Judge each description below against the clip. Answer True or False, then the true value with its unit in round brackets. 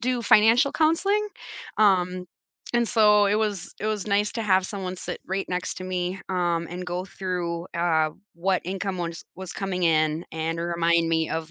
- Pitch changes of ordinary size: True (3.4 semitones)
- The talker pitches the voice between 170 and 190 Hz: True (185 Hz)